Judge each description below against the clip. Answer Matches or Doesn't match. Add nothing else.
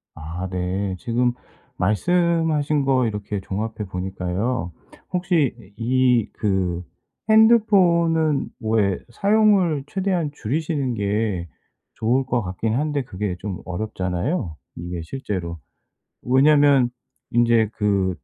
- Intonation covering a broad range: Matches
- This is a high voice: Doesn't match